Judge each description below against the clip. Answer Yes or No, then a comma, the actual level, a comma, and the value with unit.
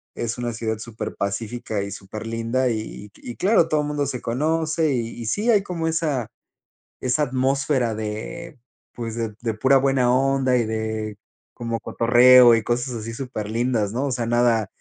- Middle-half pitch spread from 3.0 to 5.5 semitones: Yes, average, 3.4 semitones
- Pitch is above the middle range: No, low, 120 Hz